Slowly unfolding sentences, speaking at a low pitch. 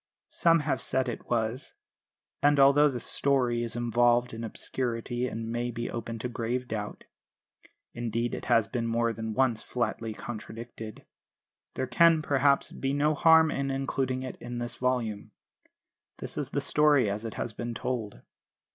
No: average, 160 wpm; low, 120 Hz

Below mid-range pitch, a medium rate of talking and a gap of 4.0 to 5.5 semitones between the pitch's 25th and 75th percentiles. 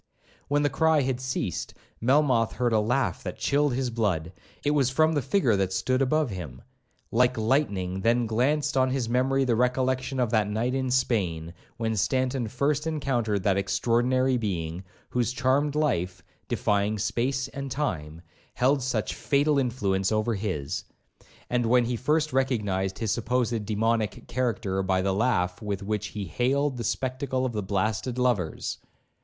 Yes: low, 120 Hz; average, 160 wpm; average, 4.3 semitones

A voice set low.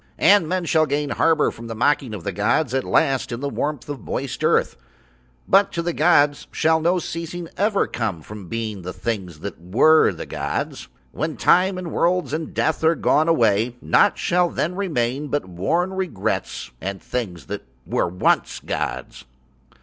No: medium, 145 Hz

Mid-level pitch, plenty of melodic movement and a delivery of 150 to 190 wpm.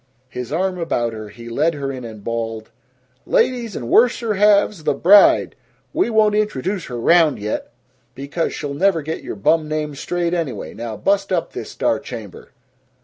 Yes: medium, 160 Hz; wide, 8.5 semitones; average, 170 wpm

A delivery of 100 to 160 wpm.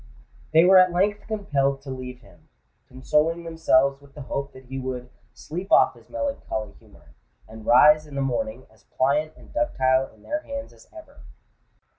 No: average, 170 wpm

